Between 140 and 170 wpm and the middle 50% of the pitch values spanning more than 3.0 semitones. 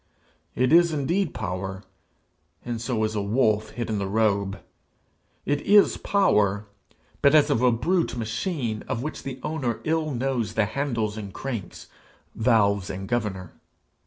Yes: average, 150 wpm; average, 5.2 semitones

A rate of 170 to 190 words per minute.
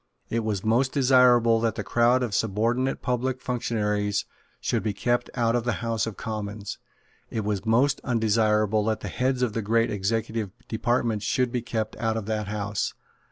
Yes: average, 175 wpm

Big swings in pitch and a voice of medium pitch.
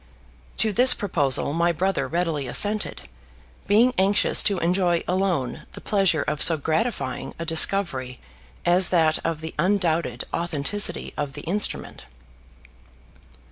No: average, 4.0 semitones; medium, 170 Hz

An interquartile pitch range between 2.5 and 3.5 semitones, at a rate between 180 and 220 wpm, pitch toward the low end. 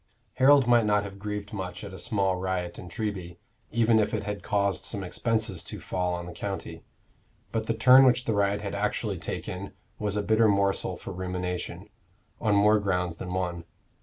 Yes: average, 2.9 semitones; average, 190 wpm; low, 100 Hz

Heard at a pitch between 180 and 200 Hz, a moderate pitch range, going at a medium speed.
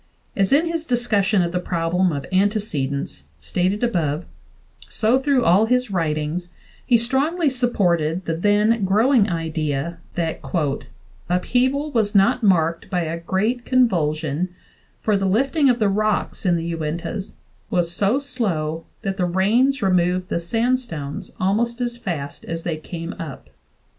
No: high, 190 Hz; wide, 6.1 semitones; average, 145 wpm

